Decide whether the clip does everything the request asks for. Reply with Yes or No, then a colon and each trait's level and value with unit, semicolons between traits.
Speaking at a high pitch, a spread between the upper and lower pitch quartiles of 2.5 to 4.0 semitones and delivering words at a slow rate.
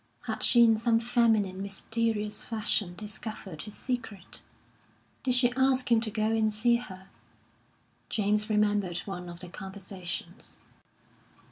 Yes: high, 215 Hz; average, 3.0 semitones; slow, 130 wpm